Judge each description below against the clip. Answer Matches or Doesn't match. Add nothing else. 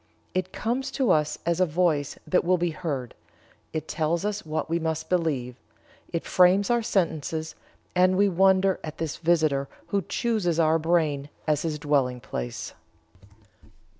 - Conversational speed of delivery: Matches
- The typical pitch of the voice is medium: Matches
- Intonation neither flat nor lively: Matches